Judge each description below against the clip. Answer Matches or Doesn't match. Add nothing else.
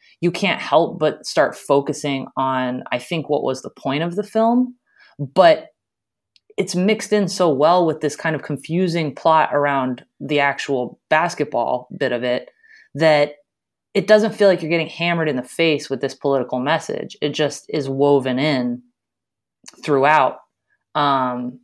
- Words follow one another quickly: Doesn't match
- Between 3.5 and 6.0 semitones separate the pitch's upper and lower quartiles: Matches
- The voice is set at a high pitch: Doesn't match